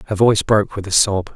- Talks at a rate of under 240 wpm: No, fast, 265 wpm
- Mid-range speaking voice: No, low, 100 Hz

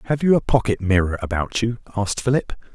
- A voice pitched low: Yes, low, 110 Hz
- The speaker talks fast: No, average, 195 wpm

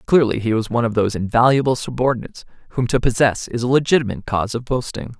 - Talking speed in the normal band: Yes, average, 195 wpm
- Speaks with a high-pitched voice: No, low, 120 Hz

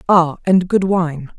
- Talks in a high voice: No, medium, 175 Hz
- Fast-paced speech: No, average, 175 wpm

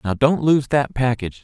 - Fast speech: Yes, fast, 210 wpm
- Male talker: Yes, male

